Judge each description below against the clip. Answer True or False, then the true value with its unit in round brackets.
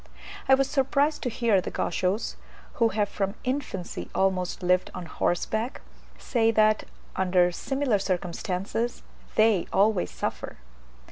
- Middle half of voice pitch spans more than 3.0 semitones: True (4.4 semitones)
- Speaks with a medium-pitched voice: False (210 Hz)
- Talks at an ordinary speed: False (125 wpm)